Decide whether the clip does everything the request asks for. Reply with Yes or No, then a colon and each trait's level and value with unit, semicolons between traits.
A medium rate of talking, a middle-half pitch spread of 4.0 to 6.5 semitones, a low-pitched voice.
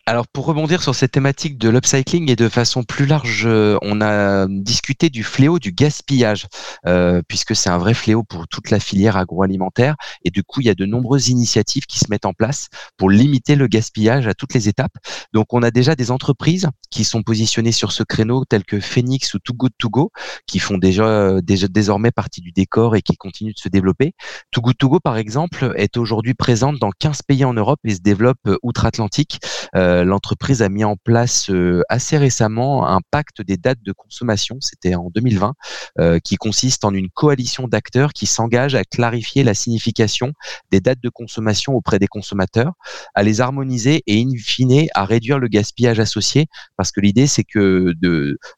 Yes: average, 195 wpm; average, 4.4 semitones; low, 115 Hz